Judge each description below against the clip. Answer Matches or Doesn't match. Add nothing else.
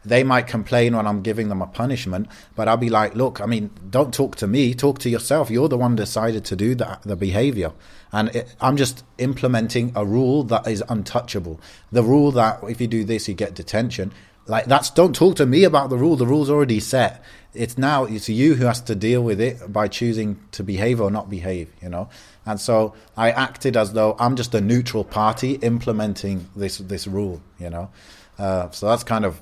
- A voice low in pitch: Matches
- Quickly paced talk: Matches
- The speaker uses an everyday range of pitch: Matches